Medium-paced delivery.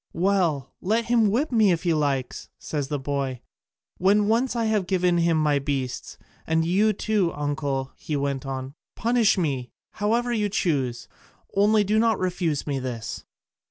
Yes: average, 160 wpm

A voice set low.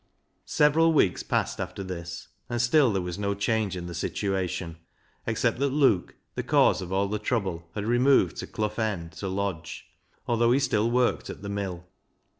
Yes: low, 100 Hz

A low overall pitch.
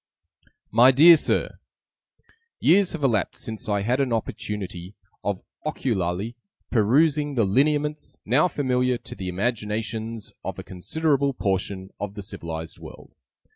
Yes: low, 115 Hz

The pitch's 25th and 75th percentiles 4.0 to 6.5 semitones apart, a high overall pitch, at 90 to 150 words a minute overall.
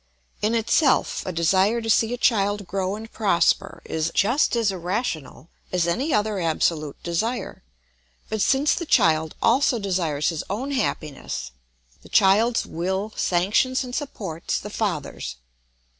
Yes: wide, 5.4 semitones; high, 200 Hz; average, 140 wpm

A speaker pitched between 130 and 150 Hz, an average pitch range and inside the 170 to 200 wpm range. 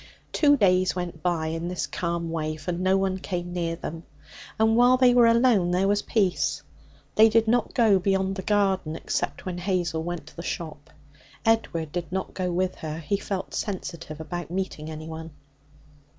No: medium, 180 Hz; average, 3.3 semitones; average, 180 wpm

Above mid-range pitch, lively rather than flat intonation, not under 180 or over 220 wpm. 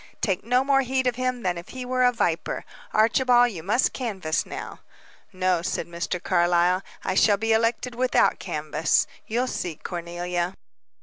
No: high, 215 Hz; wide, 5.9 semitones; average, 165 wpm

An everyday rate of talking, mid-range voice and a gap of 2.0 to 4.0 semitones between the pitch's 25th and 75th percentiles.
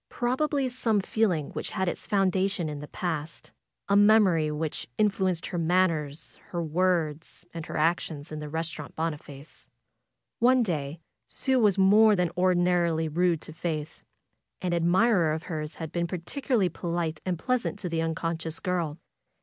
Yes: average, 155 wpm; medium, 170 Hz; average, 3.3 semitones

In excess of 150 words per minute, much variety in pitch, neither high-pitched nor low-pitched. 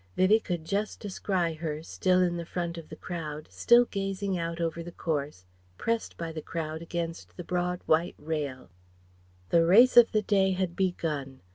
No: average, 175 wpm; average, 2.9 semitones; medium, 170 Hz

